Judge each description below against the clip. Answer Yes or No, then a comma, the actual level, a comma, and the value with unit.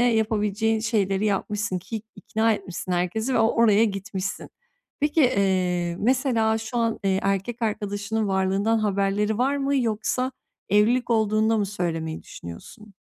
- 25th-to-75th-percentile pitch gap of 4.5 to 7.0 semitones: No, narrow, 2.6 semitones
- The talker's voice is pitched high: Yes, high, 215 Hz